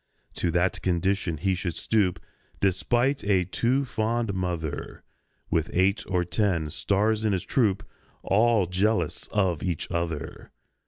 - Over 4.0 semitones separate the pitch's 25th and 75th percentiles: No, average, 3.7 semitones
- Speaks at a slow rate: Yes, slow, 130 wpm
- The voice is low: Yes, very low, 95 Hz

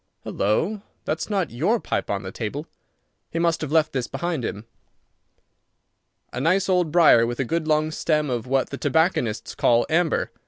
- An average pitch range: No, wide, 5.8 semitones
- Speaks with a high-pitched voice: No, medium, 155 Hz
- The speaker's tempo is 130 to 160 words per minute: No, average, 170 wpm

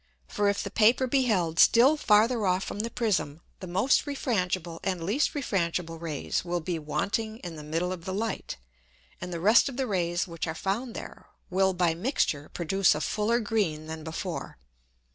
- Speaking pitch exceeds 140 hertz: Yes, medium, 185 Hz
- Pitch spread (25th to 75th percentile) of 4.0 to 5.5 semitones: Yes, average, 5.0 semitones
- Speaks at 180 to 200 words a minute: Yes, average, 185 wpm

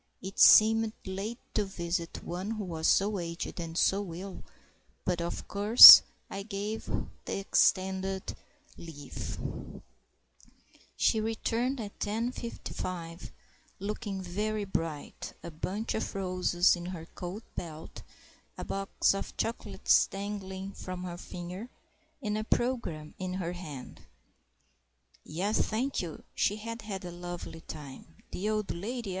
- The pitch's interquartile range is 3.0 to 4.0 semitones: Yes, average, 3.5 semitones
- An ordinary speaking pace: No, slow, 125 wpm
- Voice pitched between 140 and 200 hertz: Yes, high, 190 Hz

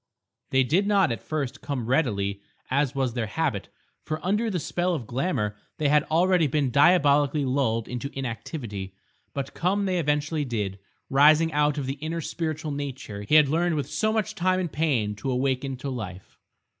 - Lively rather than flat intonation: No, average, 4.4 semitones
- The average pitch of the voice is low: No, medium, 145 Hz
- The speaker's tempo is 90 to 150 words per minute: No, average, 180 wpm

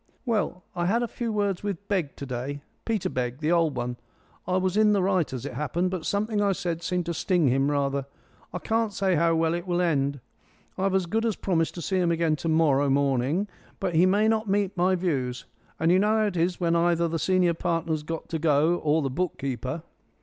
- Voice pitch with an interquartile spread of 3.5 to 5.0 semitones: Yes, average, 4.1 semitones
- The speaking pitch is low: No, medium, 170 Hz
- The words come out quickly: Yes, fast, 225 wpm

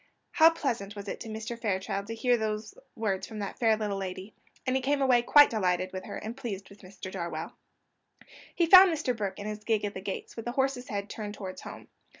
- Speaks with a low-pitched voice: No, high, 215 Hz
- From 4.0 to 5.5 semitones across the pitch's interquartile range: No, average, 3.6 semitones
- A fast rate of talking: Yes, fast, 225 wpm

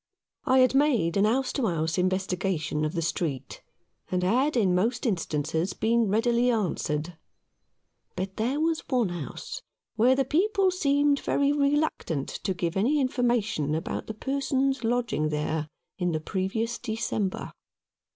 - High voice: Yes, high, 220 Hz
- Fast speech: No, average, 140 wpm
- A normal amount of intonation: No, wide, 7.1 semitones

